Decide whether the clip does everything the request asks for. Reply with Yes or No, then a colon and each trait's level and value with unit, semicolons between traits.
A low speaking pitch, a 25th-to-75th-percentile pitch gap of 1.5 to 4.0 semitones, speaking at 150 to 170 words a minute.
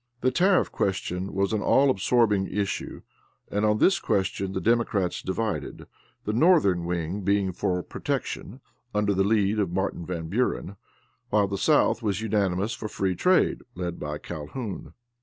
Yes: low, 100 Hz; average, 3.0 semitones; average, 155 wpm